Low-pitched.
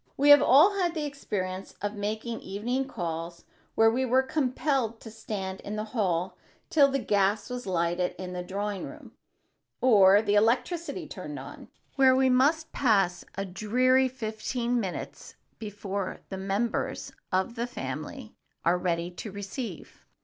No: high, 215 Hz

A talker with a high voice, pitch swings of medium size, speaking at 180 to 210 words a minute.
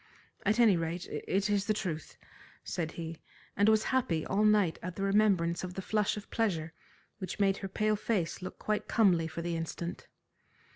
Yes: high, 195 Hz; average, 3.9 semitones; average, 185 wpm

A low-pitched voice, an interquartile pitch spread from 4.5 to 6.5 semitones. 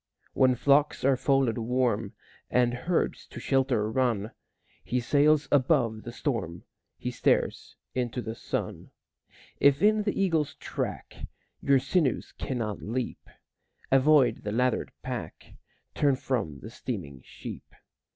No: low, 125 Hz; average, 3.6 semitones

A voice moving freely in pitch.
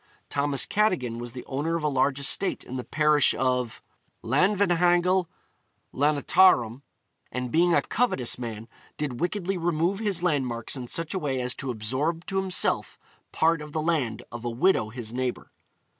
Yes: wide, 5.7 semitones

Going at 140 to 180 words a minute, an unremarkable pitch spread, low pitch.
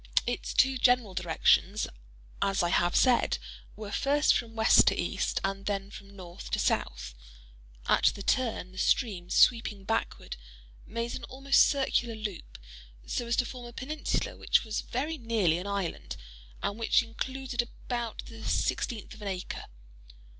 No: average, 155 wpm; average, 4.0 semitones; high, 225 Hz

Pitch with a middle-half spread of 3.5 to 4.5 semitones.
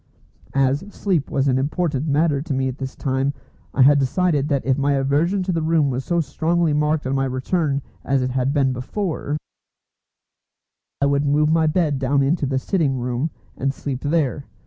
No: average, 2.9 semitones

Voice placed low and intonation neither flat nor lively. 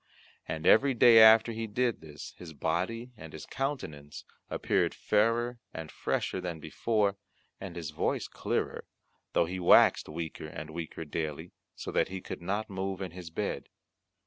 No: very low, 90 Hz; wide, 5.7 semitones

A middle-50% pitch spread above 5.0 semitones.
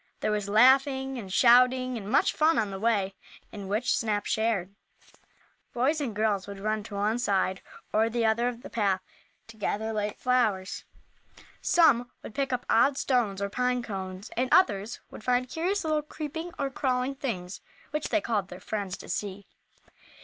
No: average, 4.0 semitones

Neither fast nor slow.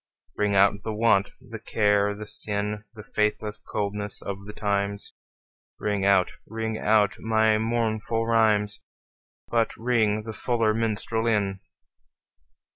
No: slow, 125 wpm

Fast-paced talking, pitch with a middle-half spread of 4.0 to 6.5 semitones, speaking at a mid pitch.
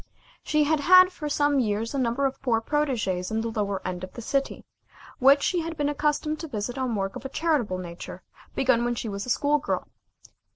No: fast, 215 wpm; average, 5.2 semitones; very high, 260 Hz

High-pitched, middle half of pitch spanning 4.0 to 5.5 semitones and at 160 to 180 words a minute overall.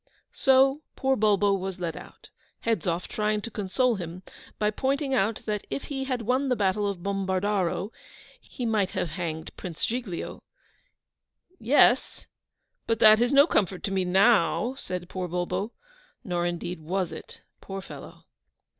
No: high, 200 Hz; average, 4.7 semitones; average, 150 wpm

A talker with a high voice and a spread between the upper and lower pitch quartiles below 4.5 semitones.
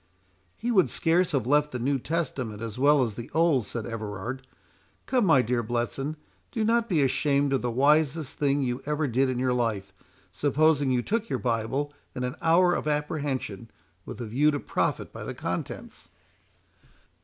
No: low, 135 Hz; average, 4.1 semitones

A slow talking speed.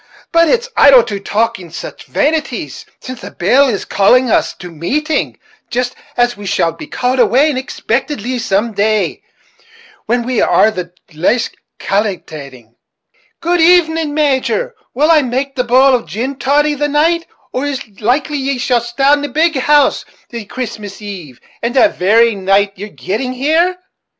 No: average, 160 wpm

